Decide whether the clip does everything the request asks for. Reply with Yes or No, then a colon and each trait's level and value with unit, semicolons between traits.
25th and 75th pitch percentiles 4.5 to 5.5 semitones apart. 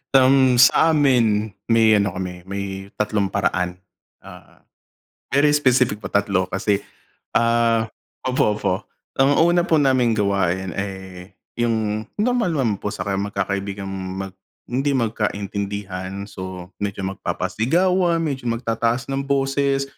Yes: average, 5.2 semitones